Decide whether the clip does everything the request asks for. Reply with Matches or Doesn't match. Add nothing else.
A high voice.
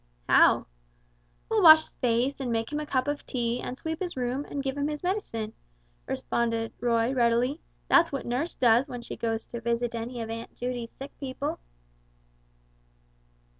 Matches